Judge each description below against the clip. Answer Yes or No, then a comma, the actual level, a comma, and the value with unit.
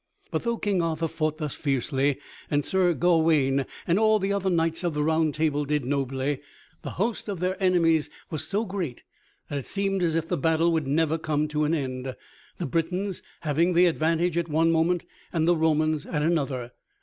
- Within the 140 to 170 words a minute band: No, average, 195 wpm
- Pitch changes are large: No, average, 2.9 semitones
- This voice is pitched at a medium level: Yes, medium, 160 Hz